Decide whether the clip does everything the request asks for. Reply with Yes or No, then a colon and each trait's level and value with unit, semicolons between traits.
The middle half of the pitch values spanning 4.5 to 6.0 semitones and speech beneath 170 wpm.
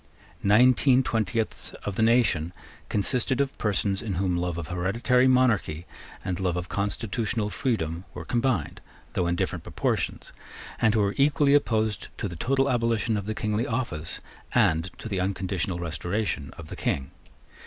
Yes: average, 5.0 semitones; average, 155 wpm